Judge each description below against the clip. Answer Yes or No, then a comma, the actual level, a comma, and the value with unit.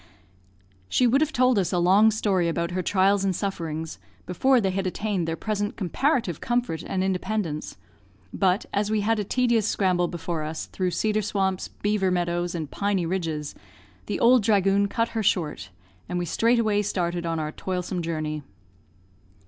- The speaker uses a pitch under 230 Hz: Yes, high, 190 Hz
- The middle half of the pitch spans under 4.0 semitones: Yes, average, 3.6 semitones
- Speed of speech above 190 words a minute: No, average, 165 wpm